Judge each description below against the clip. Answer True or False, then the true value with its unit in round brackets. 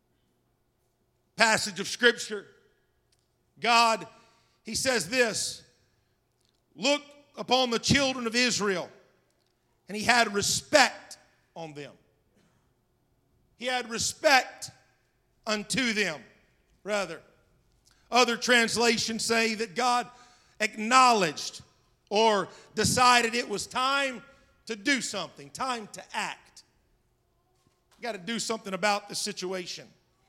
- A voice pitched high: True (215 Hz)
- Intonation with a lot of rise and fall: True (7.1 semitones)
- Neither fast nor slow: False (100 wpm)